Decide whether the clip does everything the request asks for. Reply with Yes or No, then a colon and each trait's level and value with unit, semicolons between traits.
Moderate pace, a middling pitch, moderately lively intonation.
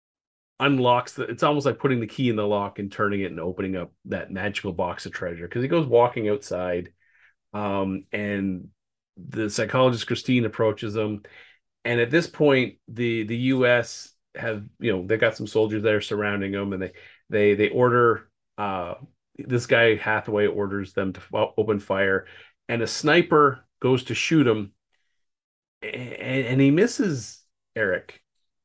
No: average, 160 wpm; low, 110 Hz; average, 3.3 semitones